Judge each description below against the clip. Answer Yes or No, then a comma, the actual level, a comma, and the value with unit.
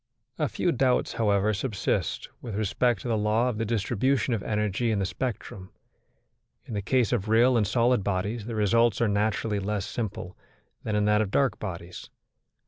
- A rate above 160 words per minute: Yes, average, 180 wpm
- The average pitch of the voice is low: Yes, low, 110 Hz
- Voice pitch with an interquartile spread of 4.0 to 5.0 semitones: No, average, 2.7 semitones